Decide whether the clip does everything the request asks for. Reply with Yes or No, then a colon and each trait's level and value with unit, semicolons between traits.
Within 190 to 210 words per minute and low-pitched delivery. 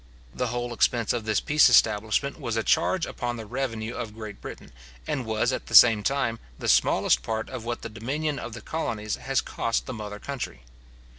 Yes: average, 200 wpm; low, 115 Hz